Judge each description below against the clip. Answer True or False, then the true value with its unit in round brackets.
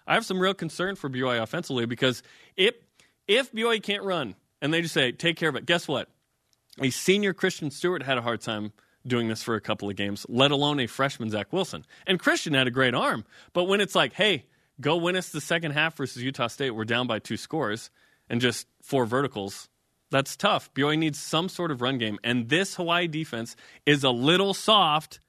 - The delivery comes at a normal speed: False (215 wpm)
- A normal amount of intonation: False (6.3 semitones)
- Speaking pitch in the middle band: True (145 Hz)